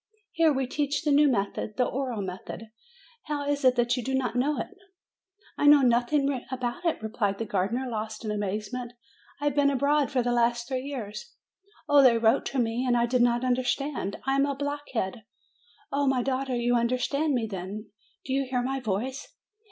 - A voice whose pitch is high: Yes, very high, 250 Hz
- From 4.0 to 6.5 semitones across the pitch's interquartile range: No, average, 3.1 semitones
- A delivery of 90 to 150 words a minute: No, average, 195 wpm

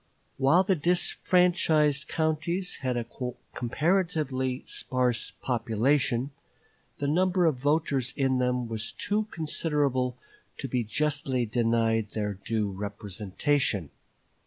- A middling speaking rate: No, slow, 105 wpm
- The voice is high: No, low, 130 Hz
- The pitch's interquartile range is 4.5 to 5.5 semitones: Yes, average, 5.1 semitones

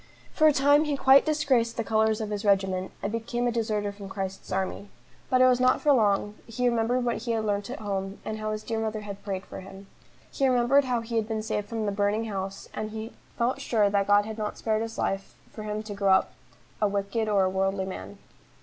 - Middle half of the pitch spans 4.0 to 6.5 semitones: No, average, 2.7 semitones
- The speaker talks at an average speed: No, fast, 240 wpm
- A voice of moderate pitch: No, high, 215 Hz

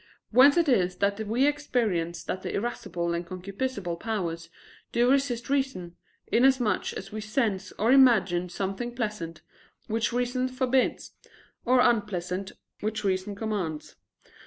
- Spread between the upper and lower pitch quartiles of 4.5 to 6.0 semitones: Yes, average, 5.3 semitones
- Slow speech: Yes, slow, 130 wpm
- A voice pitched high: Yes, high, 215 Hz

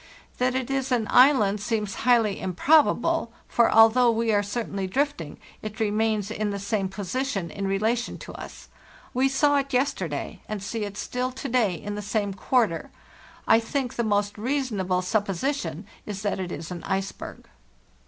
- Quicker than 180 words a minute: No, average, 170 wpm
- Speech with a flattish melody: No, average, 4.2 semitones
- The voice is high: Yes, high, 215 Hz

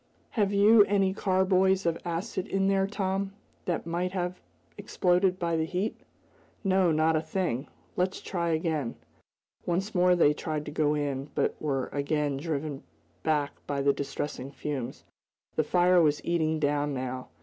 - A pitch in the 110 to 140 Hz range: No, medium, 170 Hz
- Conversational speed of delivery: Yes, average, 155 wpm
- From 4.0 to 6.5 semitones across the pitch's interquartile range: Yes, average, 4.3 semitones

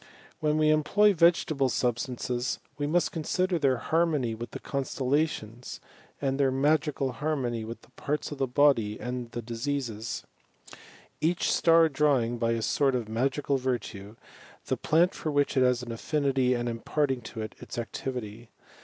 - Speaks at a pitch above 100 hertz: Yes, low, 135 Hz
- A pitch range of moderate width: Yes, average, 4.0 semitones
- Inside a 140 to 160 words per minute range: Yes, average, 155 wpm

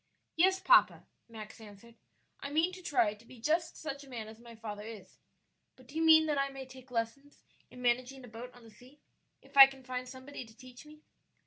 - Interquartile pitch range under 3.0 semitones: No, average, 3.8 semitones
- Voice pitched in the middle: No, very high, 255 Hz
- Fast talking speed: Yes, fast, 220 wpm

